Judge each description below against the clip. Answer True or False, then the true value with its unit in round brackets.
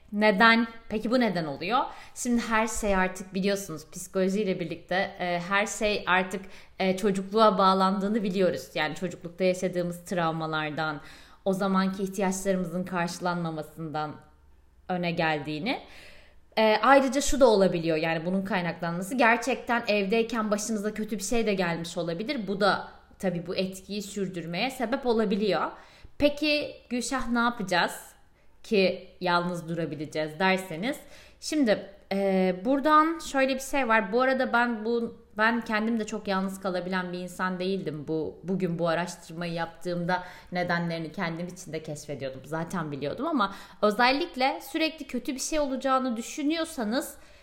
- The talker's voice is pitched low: False (195 Hz)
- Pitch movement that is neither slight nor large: True (4.8 semitones)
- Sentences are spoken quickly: False (130 wpm)